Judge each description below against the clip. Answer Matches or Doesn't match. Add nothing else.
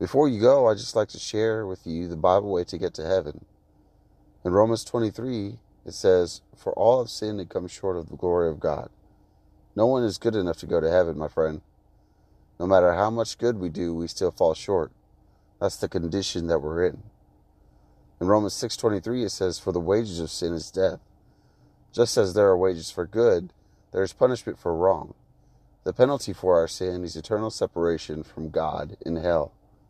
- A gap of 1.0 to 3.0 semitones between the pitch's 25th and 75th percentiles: Doesn't match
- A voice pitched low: Matches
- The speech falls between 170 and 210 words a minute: Matches